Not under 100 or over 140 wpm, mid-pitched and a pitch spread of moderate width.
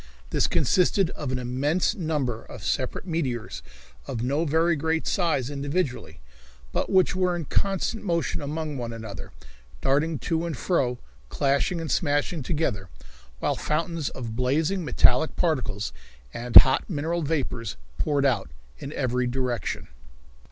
Yes: slow, 135 wpm; medium, 145 Hz; average, 4.8 semitones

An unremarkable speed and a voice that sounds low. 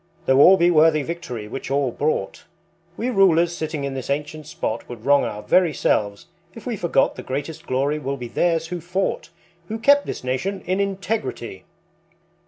No: average, 180 wpm; medium, 155 Hz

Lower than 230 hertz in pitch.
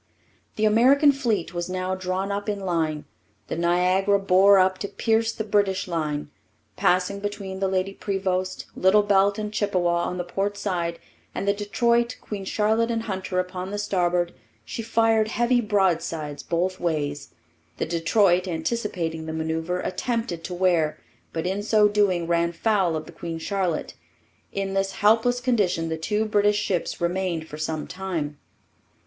Yes: high, 190 Hz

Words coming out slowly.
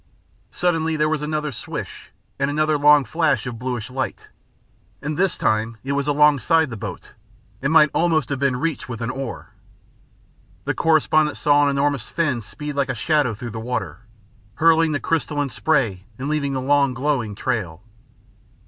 No: average, 165 wpm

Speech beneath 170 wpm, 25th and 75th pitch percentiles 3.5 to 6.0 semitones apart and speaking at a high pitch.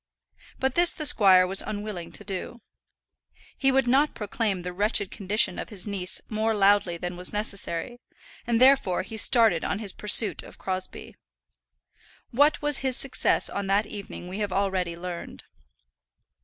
Yes: average, 155 wpm; average, 3.9 semitones; high, 205 Hz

